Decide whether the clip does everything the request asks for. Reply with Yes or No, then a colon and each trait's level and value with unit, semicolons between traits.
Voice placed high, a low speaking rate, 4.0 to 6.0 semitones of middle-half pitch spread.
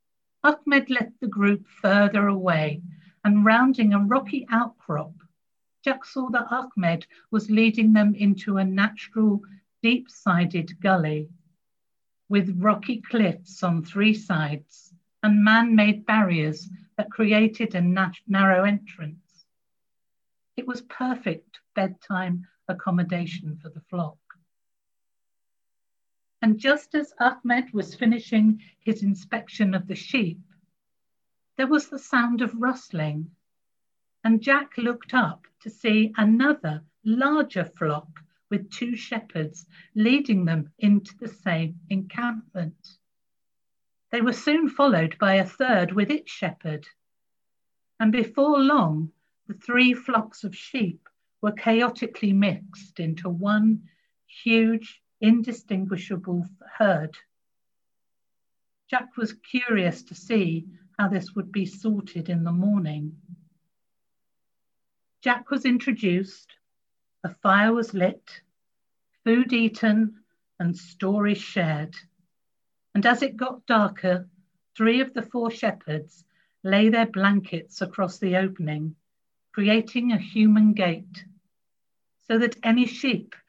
Yes: high, 205 Hz; slow, 115 wpm; average, 4.3 semitones